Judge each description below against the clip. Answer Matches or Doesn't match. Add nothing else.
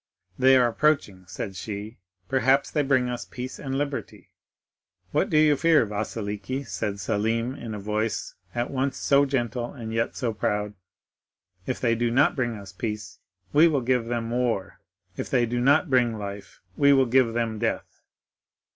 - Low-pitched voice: Matches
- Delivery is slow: Doesn't match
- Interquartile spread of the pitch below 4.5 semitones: Matches